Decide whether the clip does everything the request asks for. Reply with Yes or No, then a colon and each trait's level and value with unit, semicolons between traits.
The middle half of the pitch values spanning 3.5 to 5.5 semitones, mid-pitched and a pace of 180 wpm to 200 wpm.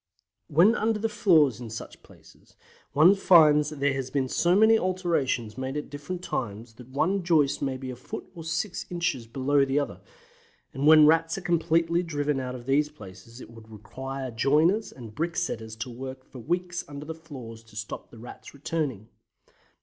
Yes: average, 4.8 semitones; medium, 145 Hz; average, 185 wpm